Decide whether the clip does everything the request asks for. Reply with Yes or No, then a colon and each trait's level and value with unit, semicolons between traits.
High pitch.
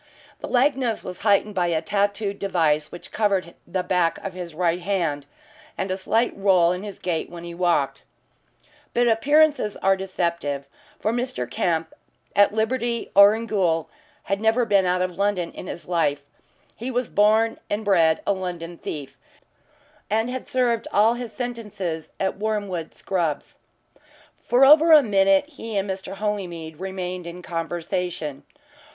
Yes: high, 195 Hz